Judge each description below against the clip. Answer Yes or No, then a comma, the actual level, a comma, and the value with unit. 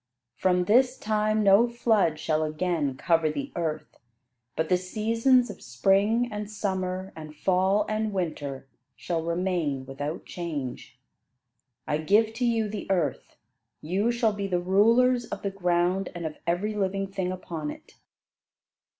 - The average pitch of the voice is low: No, medium, 185 Hz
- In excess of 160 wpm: No, average, 145 wpm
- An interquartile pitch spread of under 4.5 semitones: No, average, 4.8 semitones